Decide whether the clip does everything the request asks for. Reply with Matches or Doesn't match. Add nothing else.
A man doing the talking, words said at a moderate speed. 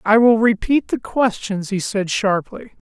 Matches